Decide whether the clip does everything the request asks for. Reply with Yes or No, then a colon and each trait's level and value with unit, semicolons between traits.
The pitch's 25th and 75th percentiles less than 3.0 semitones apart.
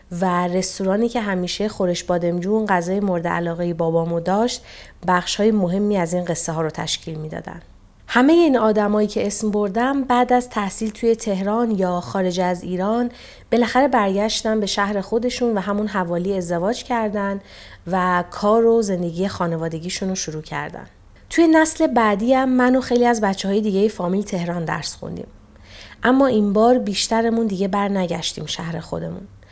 No: average, 4.3 semitones